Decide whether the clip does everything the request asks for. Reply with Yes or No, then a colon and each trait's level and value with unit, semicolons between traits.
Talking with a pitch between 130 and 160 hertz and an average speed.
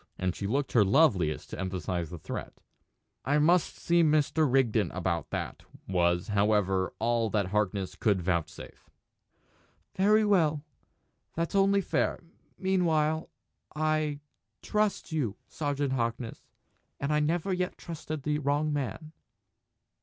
No: medium, 140 Hz; slow, 125 wpm